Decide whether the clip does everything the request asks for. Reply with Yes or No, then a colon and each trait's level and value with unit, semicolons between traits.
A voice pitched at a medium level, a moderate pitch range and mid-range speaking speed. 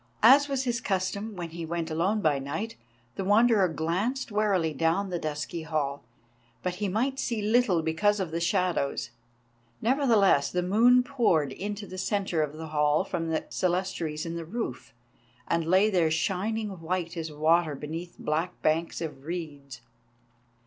Yes: medium, 175 Hz; average, 4.6 semitones; average, 160 wpm